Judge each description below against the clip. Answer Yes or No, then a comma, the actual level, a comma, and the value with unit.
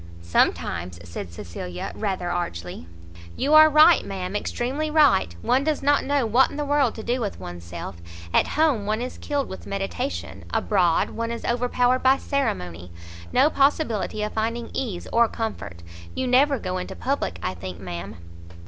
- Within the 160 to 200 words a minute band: Yes, average, 165 wpm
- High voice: Yes, high, 225 Hz